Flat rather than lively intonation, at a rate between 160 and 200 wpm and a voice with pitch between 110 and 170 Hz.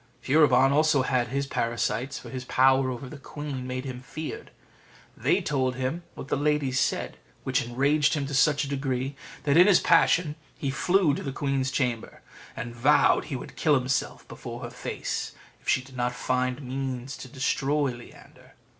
Yes: narrow, 2.3 semitones; average, 180 wpm; low, 135 Hz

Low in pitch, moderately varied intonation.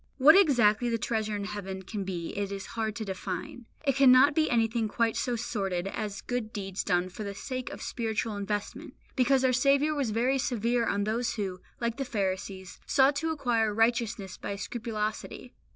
No: high, 225 Hz; average, 3.6 semitones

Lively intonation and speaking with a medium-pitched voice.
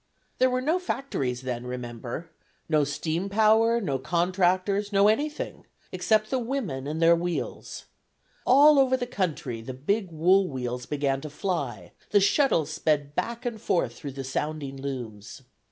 Yes: wide, 8.0 semitones; medium, 170 Hz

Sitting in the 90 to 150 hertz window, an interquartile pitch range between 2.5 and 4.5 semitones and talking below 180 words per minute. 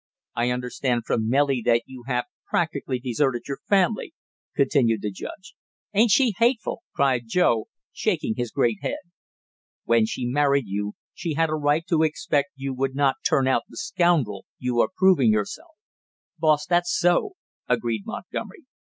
No: low, 135 Hz; wide, 5.4 semitones; average, 155 wpm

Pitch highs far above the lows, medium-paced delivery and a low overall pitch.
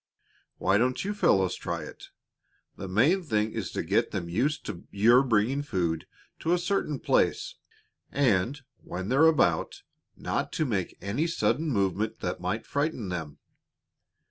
Yes: wide, 7.3 semitones; average, 150 wpm; low, 110 Hz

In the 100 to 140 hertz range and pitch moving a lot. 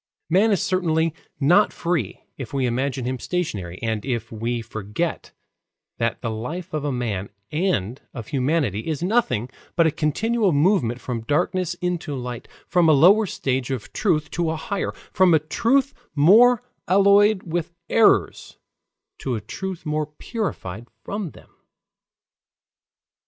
No: medium, 155 Hz; wide, 7.2 semitones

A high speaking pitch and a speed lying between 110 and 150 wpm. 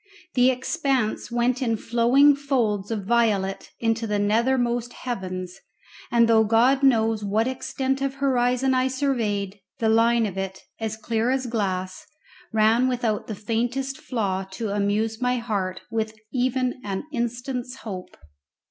Yes: high, 230 Hz; average, 140 wpm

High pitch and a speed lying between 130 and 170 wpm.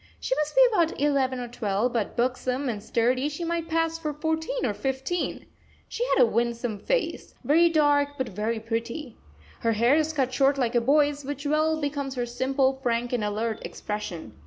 No: very high, 265 Hz; average, 185 wpm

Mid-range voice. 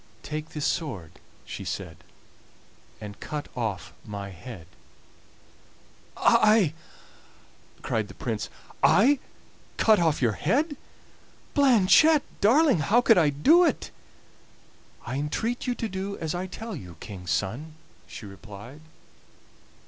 Yes: medium, 155 Hz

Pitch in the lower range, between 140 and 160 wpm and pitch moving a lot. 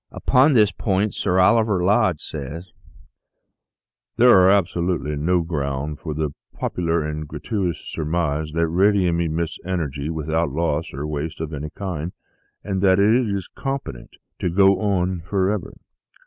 No: very low, 85 Hz; average, 150 wpm; average, 4.2 semitones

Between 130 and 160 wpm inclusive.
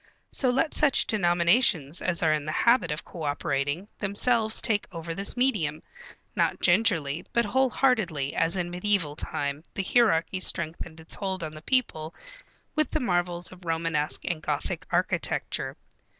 Yes: average, 150 wpm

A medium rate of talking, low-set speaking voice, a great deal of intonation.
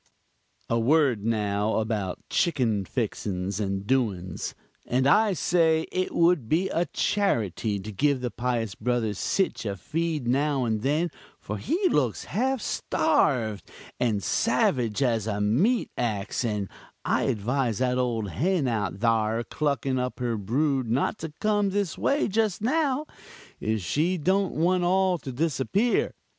Yes: average, 145 wpm; low, 125 Hz; wide, 7.7 semitones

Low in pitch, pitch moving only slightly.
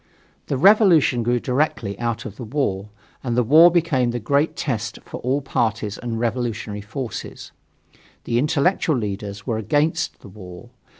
No: low, 120 Hz; average, 4.9 semitones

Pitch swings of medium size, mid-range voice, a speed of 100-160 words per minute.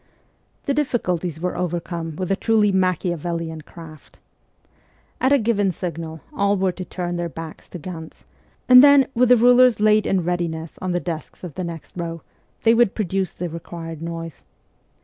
No: average, 3.9 semitones; medium, 180 Hz; average, 170 wpm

